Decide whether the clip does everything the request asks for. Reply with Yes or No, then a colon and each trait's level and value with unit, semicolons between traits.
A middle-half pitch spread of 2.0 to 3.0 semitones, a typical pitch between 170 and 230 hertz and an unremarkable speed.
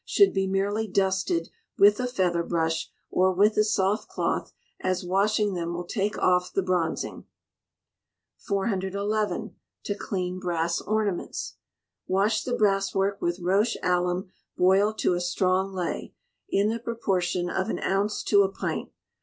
Yes: narrow, 2.4 semitones; high, 190 Hz; average, 145 wpm